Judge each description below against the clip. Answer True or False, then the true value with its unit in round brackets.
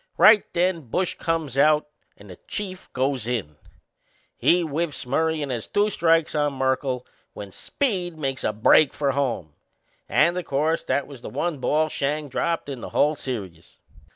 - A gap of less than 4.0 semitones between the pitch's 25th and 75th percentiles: False (4.3 semitones)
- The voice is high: False (145 Hz)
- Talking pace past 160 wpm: True (170 wpm)